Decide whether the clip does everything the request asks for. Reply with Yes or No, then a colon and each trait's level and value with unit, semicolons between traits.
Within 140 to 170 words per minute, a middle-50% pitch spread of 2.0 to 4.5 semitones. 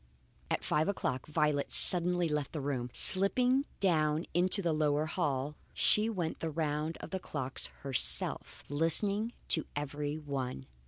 Yes: average, 145 wpm; average, 3.6 semitones